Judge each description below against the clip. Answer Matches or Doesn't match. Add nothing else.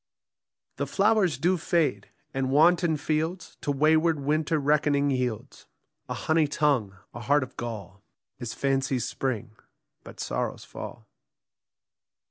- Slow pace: Matches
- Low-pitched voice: Doesn't match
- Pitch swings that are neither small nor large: Matches